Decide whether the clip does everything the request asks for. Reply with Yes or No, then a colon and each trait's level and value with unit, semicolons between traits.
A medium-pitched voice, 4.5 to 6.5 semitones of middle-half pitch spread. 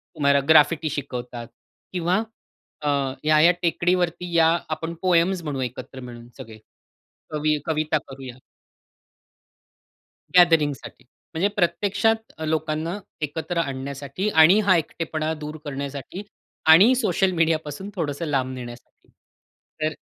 No: medium, 155 Hz; average, 3.6 semitones